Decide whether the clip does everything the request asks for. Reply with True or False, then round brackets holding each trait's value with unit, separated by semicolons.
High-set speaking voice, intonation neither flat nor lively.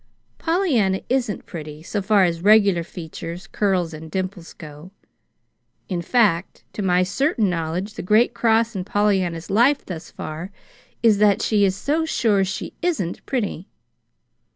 True (195 Hz; 4.2 semitones)